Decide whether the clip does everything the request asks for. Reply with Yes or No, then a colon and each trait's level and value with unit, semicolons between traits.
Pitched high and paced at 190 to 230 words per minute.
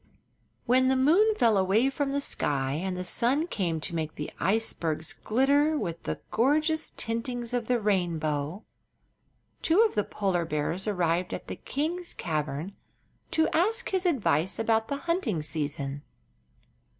No: high, 215 Hz; average, 150 wpm